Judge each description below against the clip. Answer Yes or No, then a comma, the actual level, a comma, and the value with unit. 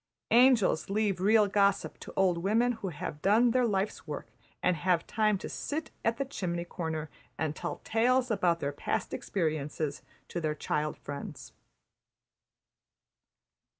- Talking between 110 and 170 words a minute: Yes, average, 145 wpm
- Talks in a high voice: Yes, high, 195 Hz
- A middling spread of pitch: No, wide, 5.7 semitones